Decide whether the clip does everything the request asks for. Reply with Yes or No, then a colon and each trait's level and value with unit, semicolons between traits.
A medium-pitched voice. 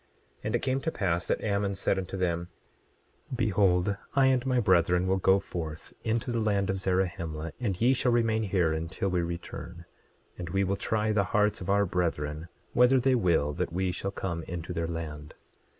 No: very low, 95 Hz